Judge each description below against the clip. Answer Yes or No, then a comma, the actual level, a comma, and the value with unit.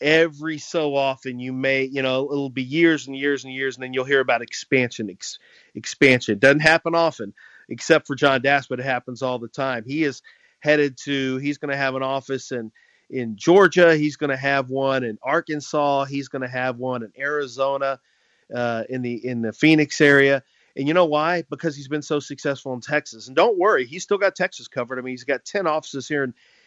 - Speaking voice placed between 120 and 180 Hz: Yes, medium, 140 Hz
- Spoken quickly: Yes, fast, 215 wpm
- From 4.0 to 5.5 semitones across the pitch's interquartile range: No, narrow, 2.5 semitones